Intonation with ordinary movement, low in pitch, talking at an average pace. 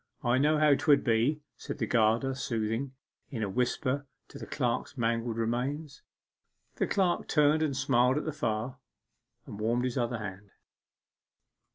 Yes: average, 3.9 semitones; low, 125 Hz; average, 155 wpm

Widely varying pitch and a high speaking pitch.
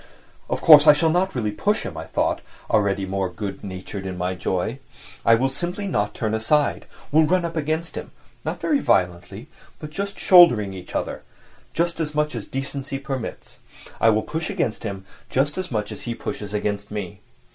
No: wide, 7.9 semitones; low, 120 Hz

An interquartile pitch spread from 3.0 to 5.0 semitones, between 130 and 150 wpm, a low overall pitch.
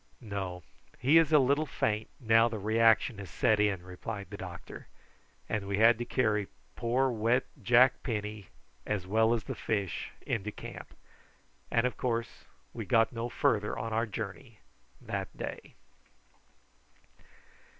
No: narrow, 2.5 semitones; average, 145 wpm; low, 110 Hz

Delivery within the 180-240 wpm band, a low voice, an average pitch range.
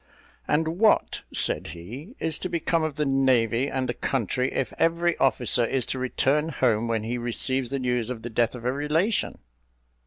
Yes: average, 185 wpm; low, 130 Hz; average, 4.1 semitones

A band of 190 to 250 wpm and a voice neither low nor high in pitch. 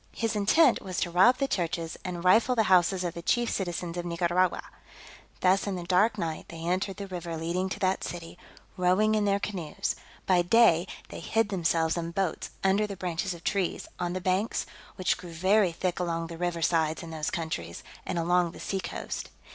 Yes: average, 200 wpm; medium, 180 Hz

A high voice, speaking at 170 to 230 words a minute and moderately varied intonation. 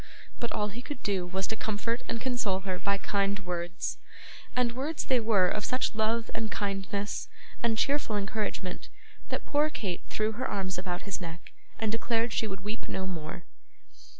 Yes: high, 210 Hz; average, 180 wpm; average, 3.3 semitones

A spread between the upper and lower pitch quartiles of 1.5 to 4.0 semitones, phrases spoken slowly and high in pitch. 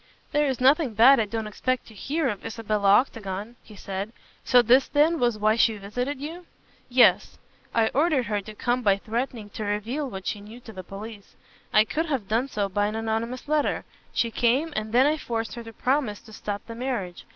No: average, 3.7 semitones; fast, 205 wpm; high, 230 Hz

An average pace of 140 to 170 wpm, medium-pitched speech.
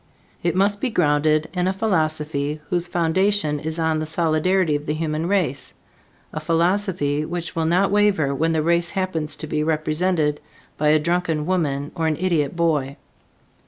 Yes: average, 165 wpm; medium, 160 Hz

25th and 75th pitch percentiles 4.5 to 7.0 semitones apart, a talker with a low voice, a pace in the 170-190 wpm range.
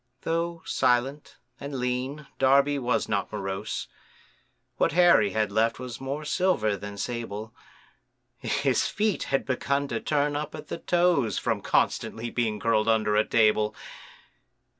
No: average, 5.0 semitones; low, 125 Hz; average, 140 wpm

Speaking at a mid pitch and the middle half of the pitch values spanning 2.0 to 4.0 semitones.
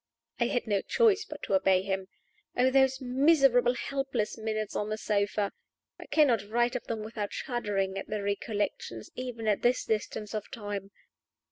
No: high, 220 Hz; average, 3.5 semitones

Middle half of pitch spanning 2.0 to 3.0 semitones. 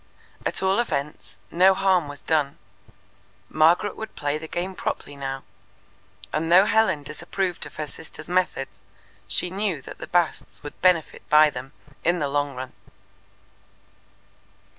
No: average, 4.2 semitones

